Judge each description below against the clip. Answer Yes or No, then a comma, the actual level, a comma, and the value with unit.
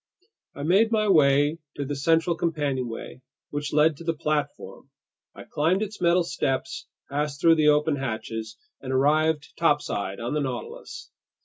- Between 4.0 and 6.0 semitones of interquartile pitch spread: No, average, 3.0 semitones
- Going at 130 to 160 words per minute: Yes, average, 150 wpm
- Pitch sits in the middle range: Yes, medium, 150 Hz